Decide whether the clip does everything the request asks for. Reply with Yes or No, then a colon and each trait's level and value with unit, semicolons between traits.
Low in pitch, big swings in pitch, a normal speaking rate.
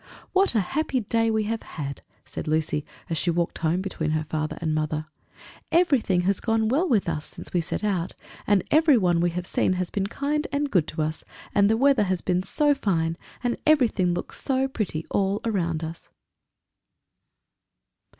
No: high, 190 Hz; wide, 6.2 semitones; average, 180 wpm